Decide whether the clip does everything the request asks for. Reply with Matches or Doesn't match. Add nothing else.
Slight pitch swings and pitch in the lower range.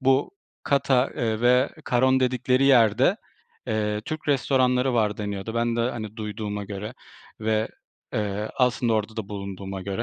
Doesn't match